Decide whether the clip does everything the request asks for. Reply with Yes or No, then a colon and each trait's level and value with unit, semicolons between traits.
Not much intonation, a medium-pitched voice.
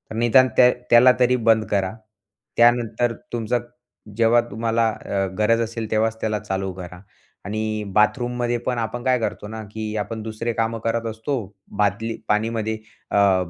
No: narrow, 1.8 semitones; low, 110 Hz